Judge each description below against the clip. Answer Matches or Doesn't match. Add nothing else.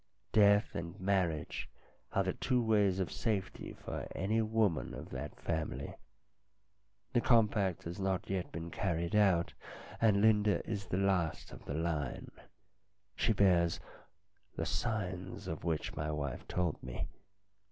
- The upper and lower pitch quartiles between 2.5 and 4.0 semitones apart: Matches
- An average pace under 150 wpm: Matches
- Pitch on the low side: Matches